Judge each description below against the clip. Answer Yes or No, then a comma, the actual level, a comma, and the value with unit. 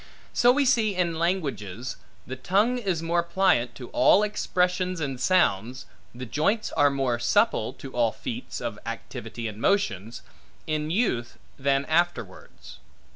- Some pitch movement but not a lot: No, wide, 7.5 semitones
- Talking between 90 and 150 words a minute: Yes, average, 140 wpm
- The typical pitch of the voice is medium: Yes, medium, 155 Hz